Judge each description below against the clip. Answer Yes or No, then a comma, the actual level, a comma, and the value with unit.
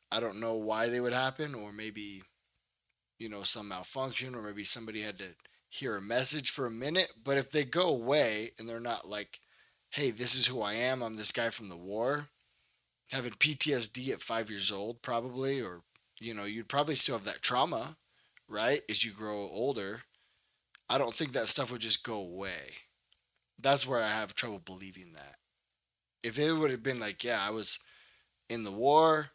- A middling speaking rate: Yes, average, 190 wpm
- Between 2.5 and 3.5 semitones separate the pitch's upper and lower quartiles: No, average, 4.1 semitones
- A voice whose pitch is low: Yes, low, 115 Hz